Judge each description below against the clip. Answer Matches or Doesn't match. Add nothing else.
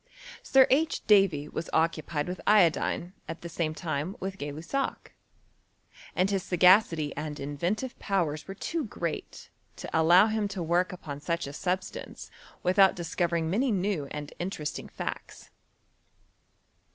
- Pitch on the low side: Doesn't match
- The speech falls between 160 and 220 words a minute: Doesn't match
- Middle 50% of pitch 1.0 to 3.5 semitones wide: Doesn't match